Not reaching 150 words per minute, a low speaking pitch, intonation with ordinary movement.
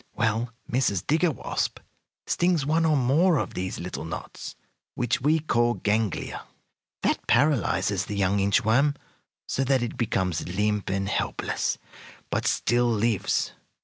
No: average, 140 wpm; low, 120 Hz; wide, 5.9 semitones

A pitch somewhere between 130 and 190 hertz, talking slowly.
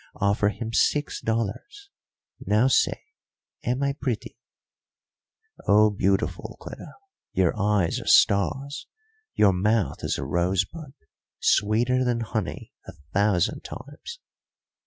No: low, 110 Hz; slow, 110 wpm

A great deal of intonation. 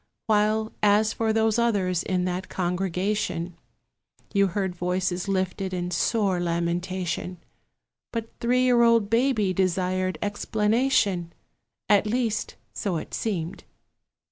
No: average, 3.3 semitones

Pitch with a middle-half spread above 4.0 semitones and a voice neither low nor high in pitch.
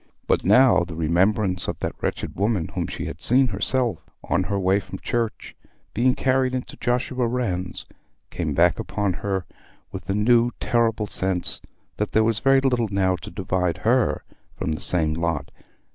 No: average, 4.8 semitones; low, 105 Hz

